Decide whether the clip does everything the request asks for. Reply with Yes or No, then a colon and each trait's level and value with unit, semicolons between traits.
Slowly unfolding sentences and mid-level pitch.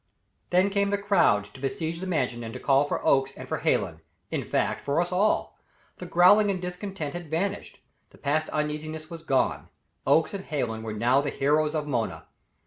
No: average, 195 wpm; medium, 155 Hz